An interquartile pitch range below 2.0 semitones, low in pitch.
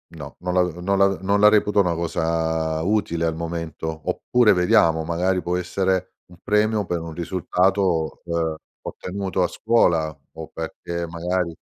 No: narrow, 2.5 semitones; very low, 85 Hz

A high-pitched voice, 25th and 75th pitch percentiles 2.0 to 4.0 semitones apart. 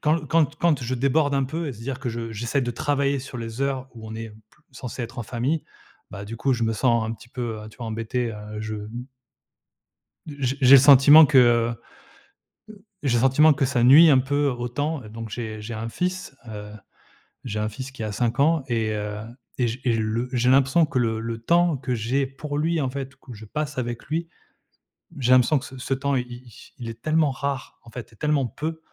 No: low, 125 Hz; average, 3.5 semitones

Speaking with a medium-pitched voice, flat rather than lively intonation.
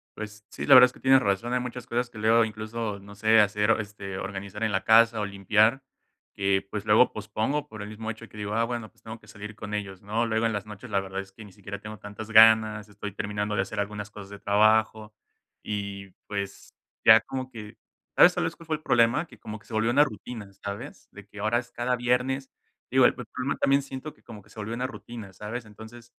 No: low, 110 Hz; narrow, 2.3 semitones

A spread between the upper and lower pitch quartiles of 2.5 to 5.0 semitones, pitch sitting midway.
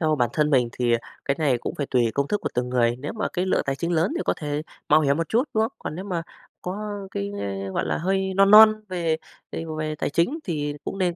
No: wide, 5.5 semitones; medium, 155 Hz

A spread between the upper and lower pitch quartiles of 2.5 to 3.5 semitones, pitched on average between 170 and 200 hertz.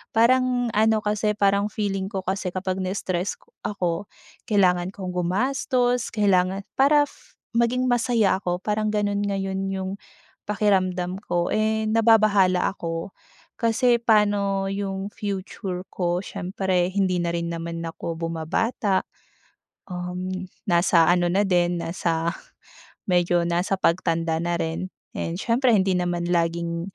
Yes: average, 3.1 semitones; high, 190 Hz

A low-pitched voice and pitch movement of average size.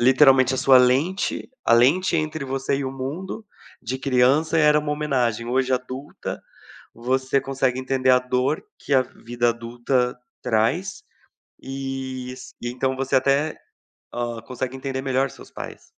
No: low, 130 Hz; narrow, 1.5 semitones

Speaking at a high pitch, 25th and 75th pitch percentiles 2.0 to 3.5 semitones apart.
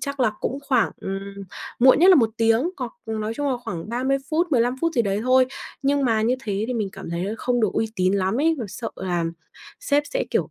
No: high, 235 Hz; average, 5.0 semitones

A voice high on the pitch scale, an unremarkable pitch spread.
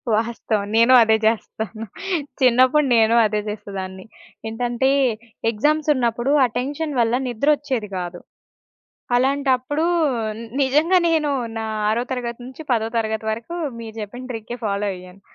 Yes: high, 235 Hz; average, 3.3 semitones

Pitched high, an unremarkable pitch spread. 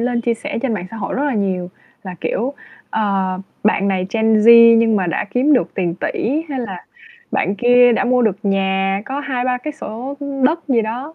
Yes: high, 230 Hz; average, 4.4 semitones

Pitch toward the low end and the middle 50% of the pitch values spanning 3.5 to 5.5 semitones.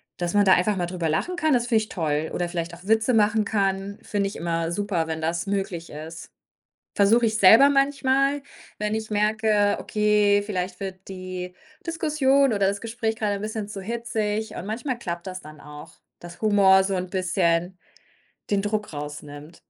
No: high, 200 Hz; average, 3.8 semitones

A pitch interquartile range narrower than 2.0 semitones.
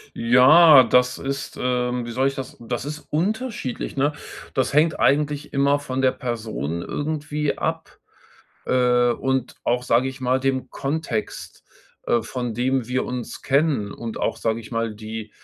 No: average, 2.9 semitones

